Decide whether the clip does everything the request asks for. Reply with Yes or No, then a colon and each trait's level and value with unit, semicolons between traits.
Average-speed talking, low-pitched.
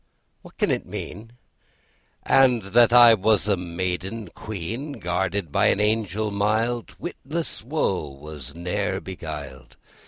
No: slow, 125 wpm; low, 100 Hz